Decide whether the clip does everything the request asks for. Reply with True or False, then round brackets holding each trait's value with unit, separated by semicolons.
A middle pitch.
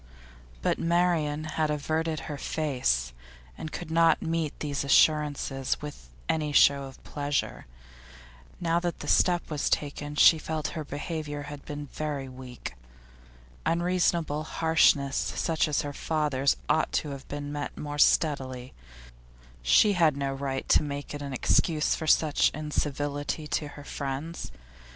True (150 Hz)